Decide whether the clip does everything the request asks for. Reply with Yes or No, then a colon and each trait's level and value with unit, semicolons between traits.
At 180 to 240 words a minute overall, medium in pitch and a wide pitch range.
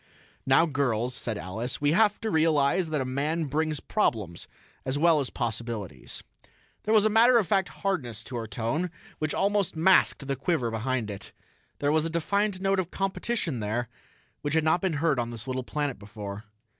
Yes: average, 185 wpm; medium, 145 Hz; wide, 6.9 semitones